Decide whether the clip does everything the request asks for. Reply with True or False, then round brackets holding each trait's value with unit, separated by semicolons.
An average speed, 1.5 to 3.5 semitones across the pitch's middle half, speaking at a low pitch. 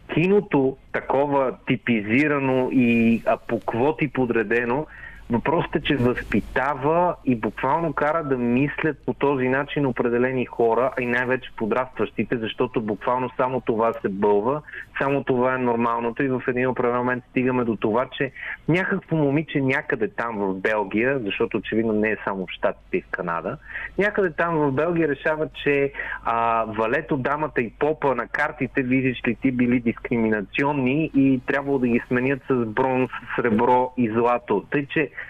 True (155 wpm; 3.2 semitones; 130 Hz)